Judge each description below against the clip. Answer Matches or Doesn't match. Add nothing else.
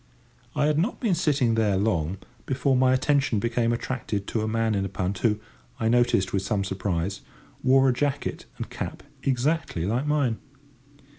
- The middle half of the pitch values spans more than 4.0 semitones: Matches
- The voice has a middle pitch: Doesn't match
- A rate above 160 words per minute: Matches